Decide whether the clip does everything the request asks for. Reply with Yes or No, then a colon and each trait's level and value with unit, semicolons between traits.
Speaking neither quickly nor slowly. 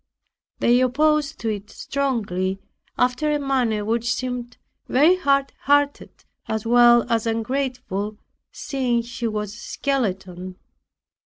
No: slow, 110 wpm